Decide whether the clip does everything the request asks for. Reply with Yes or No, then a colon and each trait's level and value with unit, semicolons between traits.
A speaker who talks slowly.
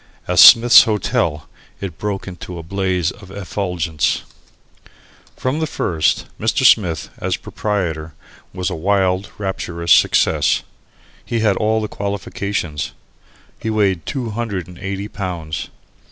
Yes: slow, 130 wpm